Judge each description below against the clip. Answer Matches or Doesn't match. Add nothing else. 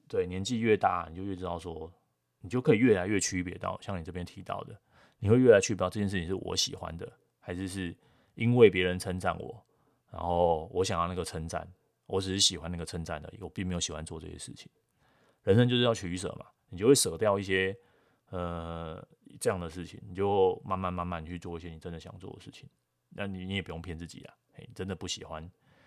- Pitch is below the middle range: Matches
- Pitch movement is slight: Matches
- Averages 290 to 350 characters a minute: Matches